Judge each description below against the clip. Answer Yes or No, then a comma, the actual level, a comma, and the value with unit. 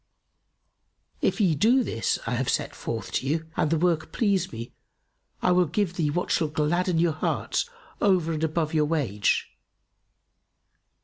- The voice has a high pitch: No, medium, 160 Hz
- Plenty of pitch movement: No, average, 3.1 semitones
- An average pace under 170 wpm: Yes, average, 160 wpm